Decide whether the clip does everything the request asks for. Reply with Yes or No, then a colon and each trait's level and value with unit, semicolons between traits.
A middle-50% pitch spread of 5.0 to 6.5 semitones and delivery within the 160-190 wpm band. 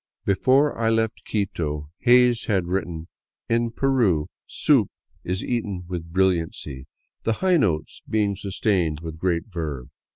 No: wide, 5.4 semitones; slow, 135 wpm